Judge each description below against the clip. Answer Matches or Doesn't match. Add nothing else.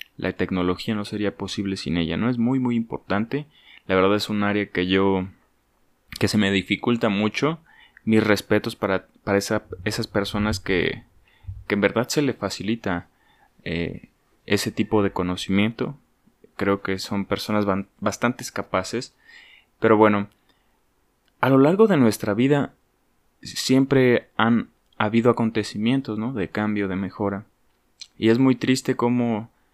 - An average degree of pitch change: Matches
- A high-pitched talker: Doesn't match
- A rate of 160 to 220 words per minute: Doesn't match